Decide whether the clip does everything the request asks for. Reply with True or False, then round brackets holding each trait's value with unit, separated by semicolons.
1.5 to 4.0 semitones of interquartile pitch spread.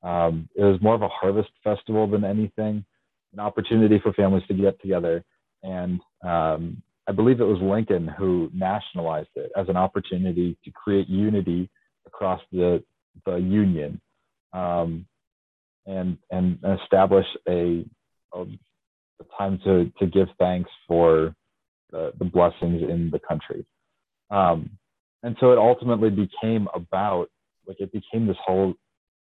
True (3.0 semitones)